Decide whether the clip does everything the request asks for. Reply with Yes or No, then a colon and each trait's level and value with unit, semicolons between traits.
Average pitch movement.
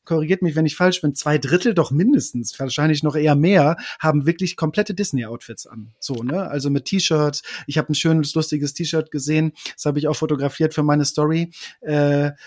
No: narrow, 2.2 semitones